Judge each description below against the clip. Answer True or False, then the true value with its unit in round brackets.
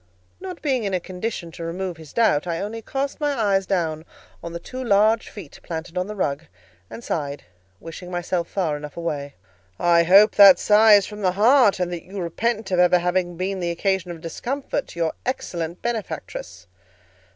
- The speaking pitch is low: False (185 Hz)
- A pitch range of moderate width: True (3.9 semitones)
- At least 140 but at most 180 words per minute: False (190 wpm)